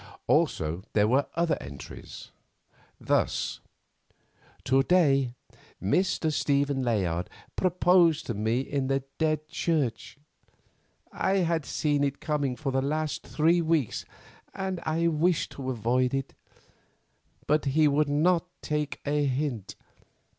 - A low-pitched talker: No, medium, 145 Hz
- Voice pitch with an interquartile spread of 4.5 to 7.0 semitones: No, average, 3.5 semitones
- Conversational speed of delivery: No, slow, 120 wpm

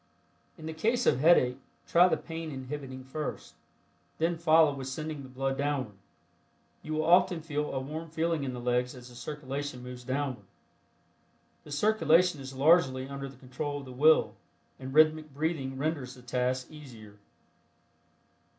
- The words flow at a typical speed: Yes, average, 160 wpm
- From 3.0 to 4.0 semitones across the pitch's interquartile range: Yes, average, 3.3 semitones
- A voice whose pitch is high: No, medium, 145 Hz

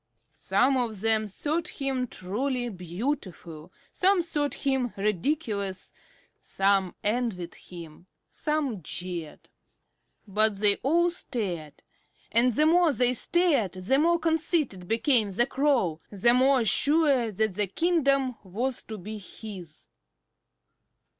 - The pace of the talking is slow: Yes, slow, 115 wpm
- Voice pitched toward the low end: No, high, 230 Hz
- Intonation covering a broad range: Yes, wide, 6.5 semitones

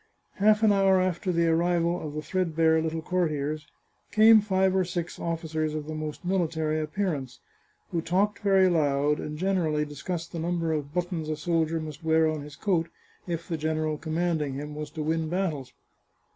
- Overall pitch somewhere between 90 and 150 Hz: No, medium, 165 Hz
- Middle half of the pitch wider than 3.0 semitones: No, narrow, 2.6 semitones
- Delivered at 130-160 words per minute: No, average, 180 wpm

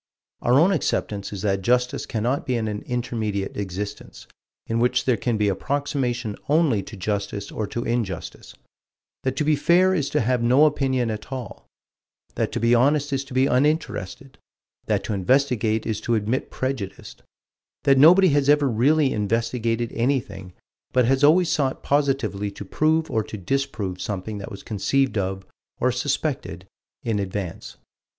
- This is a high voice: No, low, 120 Hz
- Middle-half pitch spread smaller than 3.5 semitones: No, average, 4.8 semitones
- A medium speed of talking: Yes, average, 160 wpm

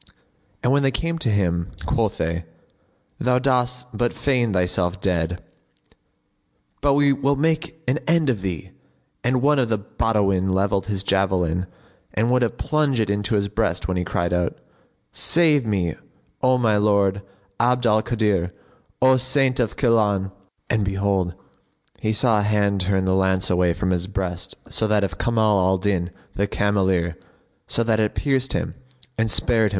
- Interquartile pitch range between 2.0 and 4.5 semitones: No, average, 4.9 semitones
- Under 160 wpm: No, average, 165 wpm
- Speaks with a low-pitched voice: Yes, low, 105 Hz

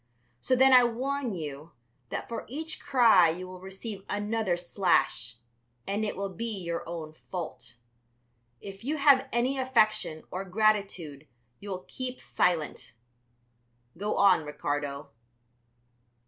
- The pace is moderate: No, slow, 130 wpm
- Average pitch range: No, wide, 5.7 semitones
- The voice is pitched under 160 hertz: No, high, 195 Hz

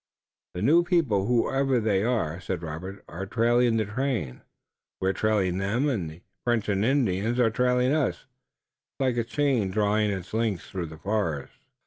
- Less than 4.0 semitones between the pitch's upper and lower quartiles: No, average, 4.7 semitones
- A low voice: Yes, low, 110 Hz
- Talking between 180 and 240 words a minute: No, average, 165 wpm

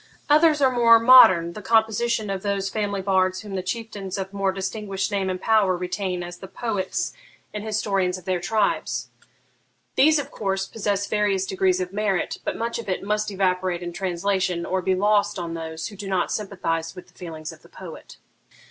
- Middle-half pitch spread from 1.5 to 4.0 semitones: Yes, narrow, 2.4 semitones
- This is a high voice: Yes, high, 195 Hz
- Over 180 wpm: Yes, average, 190 wpm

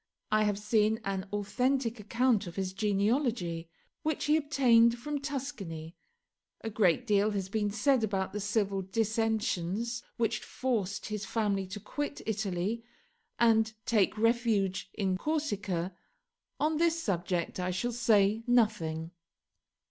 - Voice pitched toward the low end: No, high, 215 Hz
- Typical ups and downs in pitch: Yes, average, 3.5 semitones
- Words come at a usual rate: No, slow, 130 wpm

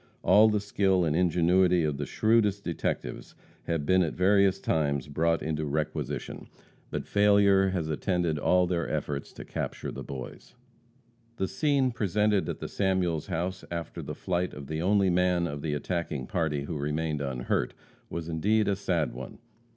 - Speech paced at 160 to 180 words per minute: Yes, average, 165 wpm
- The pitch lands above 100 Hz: No, very low, 85 Hz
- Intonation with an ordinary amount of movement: Yes, average, 4.0 semitones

